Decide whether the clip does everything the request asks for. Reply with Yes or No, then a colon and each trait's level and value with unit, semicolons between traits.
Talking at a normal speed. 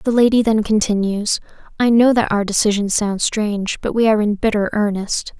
Yes: average, 190 wpm